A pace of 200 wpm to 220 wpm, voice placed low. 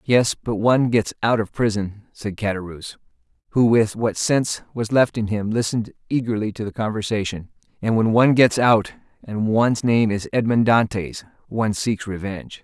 No: average, 165 wpm; low, 110 Hz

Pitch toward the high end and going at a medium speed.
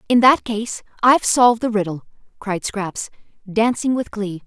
Yes: high, 220 Hz; average, 160 wpm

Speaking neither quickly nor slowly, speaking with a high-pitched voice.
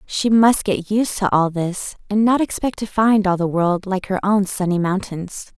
No: fast, 215 wpm; high, 195 Hz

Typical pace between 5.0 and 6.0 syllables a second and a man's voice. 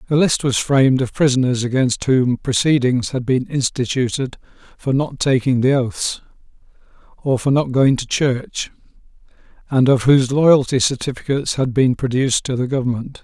Yes: 5.1 syllables/s; male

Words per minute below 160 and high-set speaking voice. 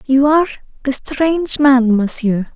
Yes: average, 140 wpm; very high, 265 Hz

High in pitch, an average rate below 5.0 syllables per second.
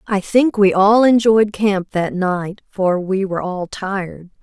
Yes: high, 195 Hz; 3.9 syllables/s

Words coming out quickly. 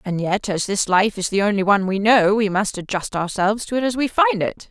Yes: fast, 270 wpm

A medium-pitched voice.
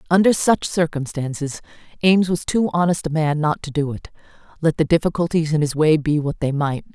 Yes: medium, 155 Hz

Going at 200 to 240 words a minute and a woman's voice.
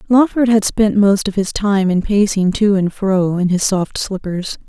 Yes: fast, 205 wpm; female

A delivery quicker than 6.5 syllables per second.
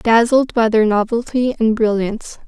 No: 4.7 syllables/s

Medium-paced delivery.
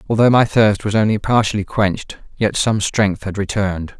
Yes: average, 180 wpm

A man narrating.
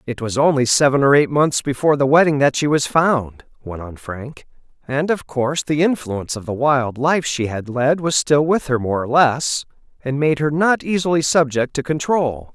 Yes: male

